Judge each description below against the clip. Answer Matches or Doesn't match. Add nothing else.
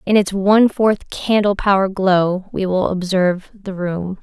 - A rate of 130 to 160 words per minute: Matches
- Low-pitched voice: Doesn't match